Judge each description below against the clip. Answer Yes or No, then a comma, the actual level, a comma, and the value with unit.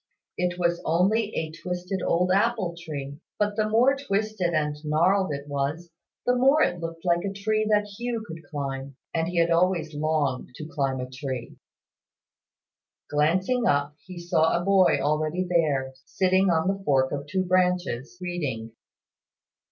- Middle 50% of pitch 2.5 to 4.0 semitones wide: No, average, 4.5 semitones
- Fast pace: No, average, 160 wpm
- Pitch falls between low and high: Yes, medium, 170 Hz